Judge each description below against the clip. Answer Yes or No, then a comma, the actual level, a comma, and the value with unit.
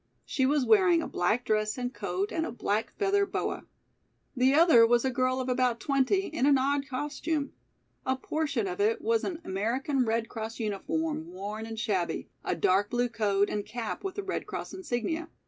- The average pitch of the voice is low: No, very high, 250 Hz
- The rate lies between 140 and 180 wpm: No, average, 190 wpm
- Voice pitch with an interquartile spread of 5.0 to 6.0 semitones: Yes, average, 5.3 semitones